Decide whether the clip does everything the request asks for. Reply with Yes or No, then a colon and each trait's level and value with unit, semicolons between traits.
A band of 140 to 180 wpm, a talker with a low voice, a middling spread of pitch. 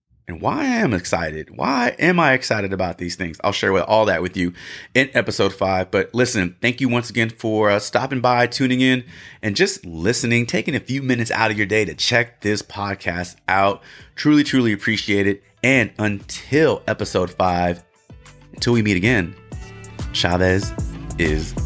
Yes: average, 170 wpm; low, 105 Hz; average, 4.7 semitones